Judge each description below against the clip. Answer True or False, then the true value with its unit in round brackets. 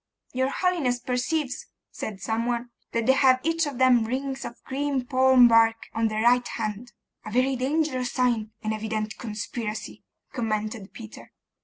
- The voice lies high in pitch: True (245 Hz)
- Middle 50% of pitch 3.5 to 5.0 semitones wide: False (2.9 semitones)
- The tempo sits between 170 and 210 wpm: False (155 wpm)